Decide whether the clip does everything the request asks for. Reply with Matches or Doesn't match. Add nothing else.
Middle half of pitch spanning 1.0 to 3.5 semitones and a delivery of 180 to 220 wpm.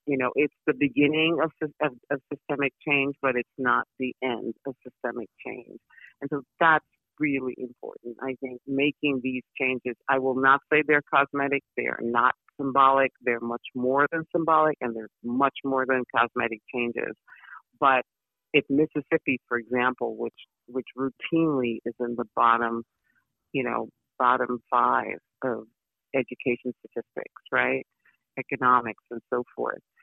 Doesn't match